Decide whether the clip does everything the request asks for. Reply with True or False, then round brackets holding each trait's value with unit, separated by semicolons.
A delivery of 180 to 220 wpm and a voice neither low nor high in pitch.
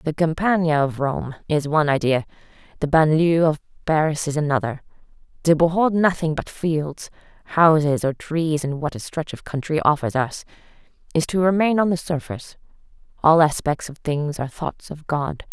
False (165 wpm; 155 Hz)